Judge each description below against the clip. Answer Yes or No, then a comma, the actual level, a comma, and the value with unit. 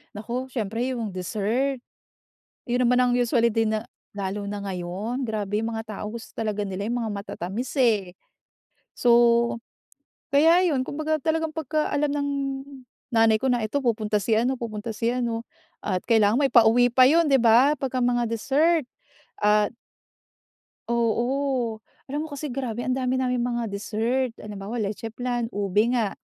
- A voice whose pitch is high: Yes, high, 235 Hz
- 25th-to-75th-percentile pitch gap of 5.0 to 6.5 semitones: No, average, 3.4 semitones